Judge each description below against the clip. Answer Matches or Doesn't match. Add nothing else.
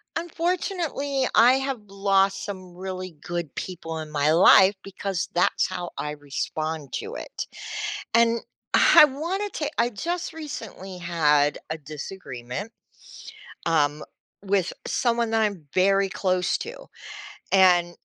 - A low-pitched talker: Doesn't match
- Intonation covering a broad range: Matches